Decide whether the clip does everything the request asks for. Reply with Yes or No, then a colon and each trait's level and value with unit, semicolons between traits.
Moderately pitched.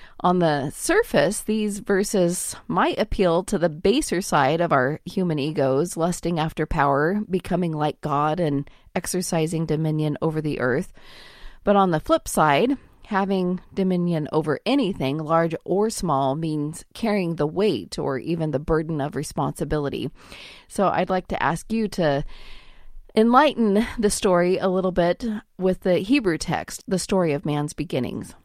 Yes: medium, 170 Hz